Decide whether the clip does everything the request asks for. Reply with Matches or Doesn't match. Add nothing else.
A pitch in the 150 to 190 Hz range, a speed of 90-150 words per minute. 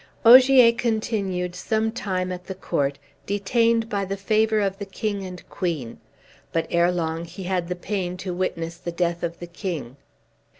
Doesn't match